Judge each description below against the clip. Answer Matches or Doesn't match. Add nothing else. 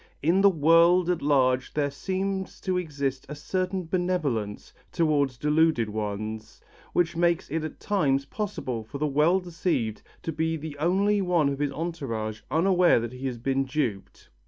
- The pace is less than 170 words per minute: Matches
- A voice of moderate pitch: Matches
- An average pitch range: Matches